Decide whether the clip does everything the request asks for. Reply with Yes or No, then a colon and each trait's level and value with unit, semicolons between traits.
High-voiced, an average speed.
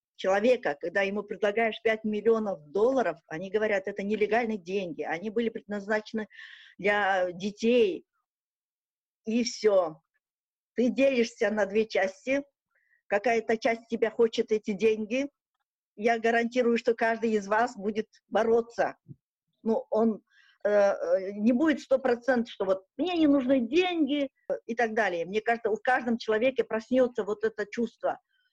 Yes: high, 225 Hz; average, 135 wpm